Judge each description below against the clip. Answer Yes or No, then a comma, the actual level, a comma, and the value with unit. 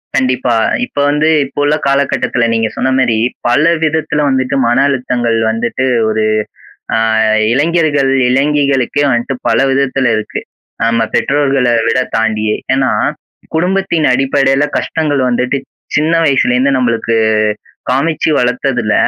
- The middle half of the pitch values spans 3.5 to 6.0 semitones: No, average, 3.1 semitones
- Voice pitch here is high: No, low, 135 Hz